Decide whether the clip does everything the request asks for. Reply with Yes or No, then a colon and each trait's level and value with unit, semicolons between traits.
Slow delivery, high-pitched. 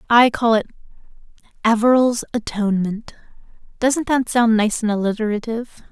Yes: slow, 110 wpm; high, 225 Hz